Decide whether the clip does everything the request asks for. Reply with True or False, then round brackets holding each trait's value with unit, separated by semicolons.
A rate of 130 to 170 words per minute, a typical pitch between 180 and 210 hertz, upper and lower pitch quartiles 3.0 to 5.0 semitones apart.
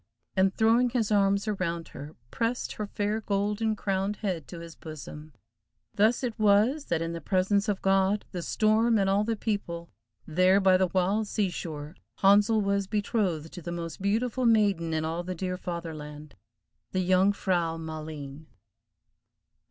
True (160 wpm; 190 Hz; 3.9 semitones)